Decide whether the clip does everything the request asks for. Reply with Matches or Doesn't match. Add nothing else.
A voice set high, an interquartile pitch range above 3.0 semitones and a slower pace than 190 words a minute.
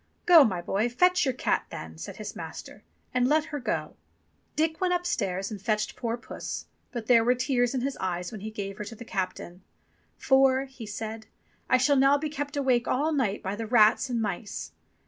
Doesn't match